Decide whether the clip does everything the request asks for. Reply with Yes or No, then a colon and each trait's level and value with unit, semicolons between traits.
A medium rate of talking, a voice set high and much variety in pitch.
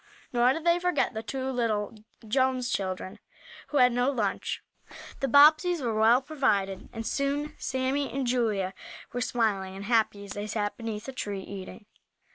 No: average, 165 wpm; high, 240 Hz; average, 4.6 semitones